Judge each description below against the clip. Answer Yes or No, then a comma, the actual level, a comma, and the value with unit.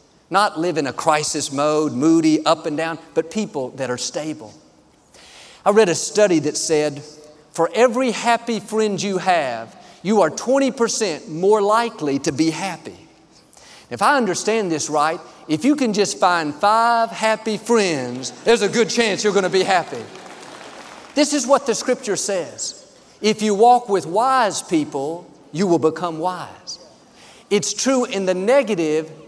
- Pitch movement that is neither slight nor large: No, wide, 6.4 semitones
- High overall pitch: Yes, high, 200 Hz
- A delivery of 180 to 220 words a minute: No, average, 160 wpm